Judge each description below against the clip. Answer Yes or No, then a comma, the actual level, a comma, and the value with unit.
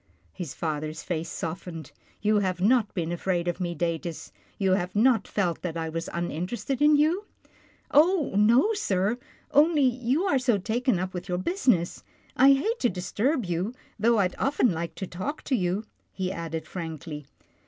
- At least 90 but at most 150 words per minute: No, average, 180 wpm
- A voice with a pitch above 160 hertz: Yes, high, 190 Hz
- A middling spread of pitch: No, wide, 6.8 semitones